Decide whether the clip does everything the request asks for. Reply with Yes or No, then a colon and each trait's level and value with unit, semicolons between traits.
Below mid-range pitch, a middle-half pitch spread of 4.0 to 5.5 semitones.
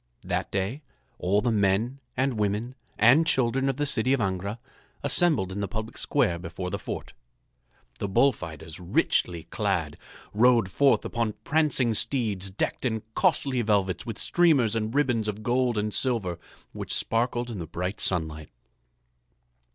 Yes: low, 110 Hz; average, 4.8 semitones